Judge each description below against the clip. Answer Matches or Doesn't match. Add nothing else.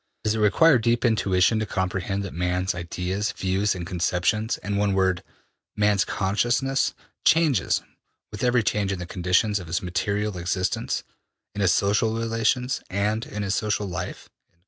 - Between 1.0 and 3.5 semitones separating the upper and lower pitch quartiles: Matches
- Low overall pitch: Matches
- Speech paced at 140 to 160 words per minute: Matches